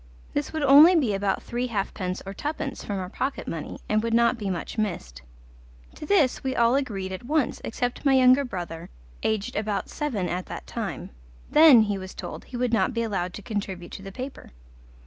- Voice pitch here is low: No, high, 220 Hz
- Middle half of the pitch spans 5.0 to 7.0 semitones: Yes, average, 5.3 semitones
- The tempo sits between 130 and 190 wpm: No, average, 200 wpm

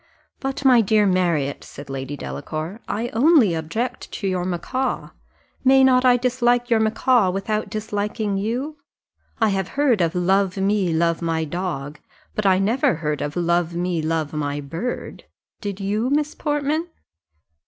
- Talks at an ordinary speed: Yes, average, 155 wpm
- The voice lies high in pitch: Yes, high, 195 Hz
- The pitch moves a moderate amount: No, wide, 6.3 semitones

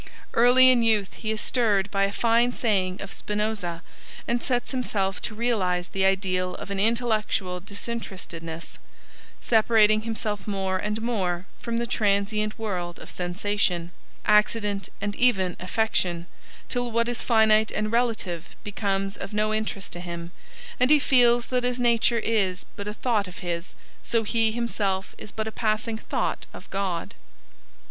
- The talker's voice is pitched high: Yes, high, 210 Hz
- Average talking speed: Yes, average, 155 wpm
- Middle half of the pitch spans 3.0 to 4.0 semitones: Yes, average, 3.3 semitones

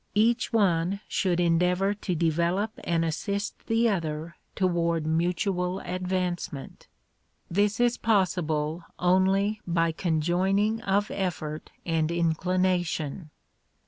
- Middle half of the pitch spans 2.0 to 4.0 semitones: Yes, average, 3.0 semitones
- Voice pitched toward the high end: No, medium, 180 Hz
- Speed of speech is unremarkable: No, slow, 100 wpm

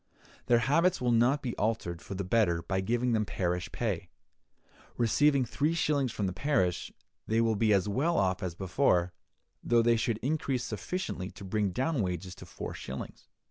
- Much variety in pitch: Yes, wide, 5.7 semitones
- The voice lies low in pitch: Yes, low, 115 Hz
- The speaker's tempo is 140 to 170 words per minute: No, average, 180 wpm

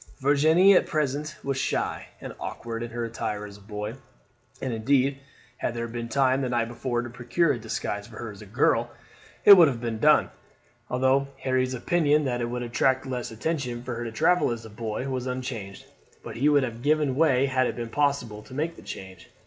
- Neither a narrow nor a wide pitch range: Yes, average, 3.3 semitones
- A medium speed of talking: No, fast, 210 wpm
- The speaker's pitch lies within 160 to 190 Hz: No, low, 125 Hz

